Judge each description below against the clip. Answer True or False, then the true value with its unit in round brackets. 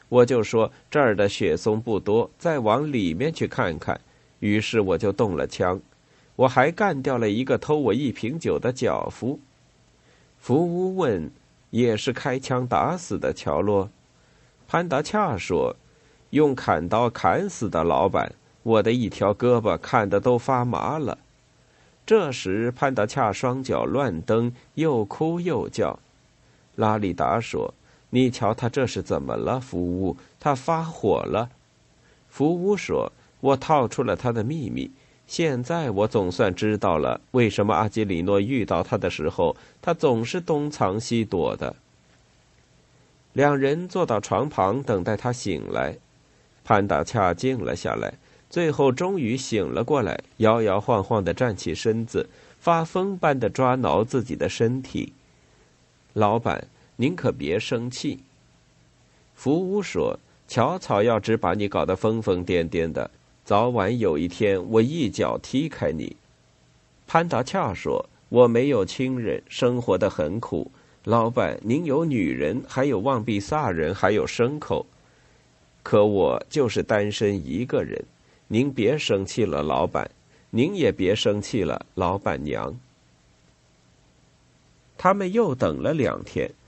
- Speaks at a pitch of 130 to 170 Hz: False (120 Hz)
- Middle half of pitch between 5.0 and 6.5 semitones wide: True (5.3 semitones)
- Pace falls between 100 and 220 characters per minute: True (200 characters per minute)